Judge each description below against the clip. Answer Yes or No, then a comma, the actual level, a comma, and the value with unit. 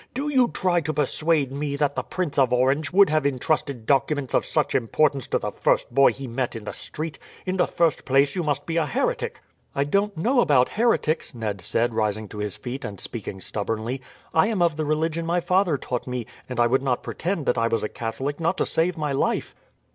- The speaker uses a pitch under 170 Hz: Yes, medium, 140 Hz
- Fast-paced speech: Yes, fast, 225 wpm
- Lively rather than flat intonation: No, average, 5.0 semitones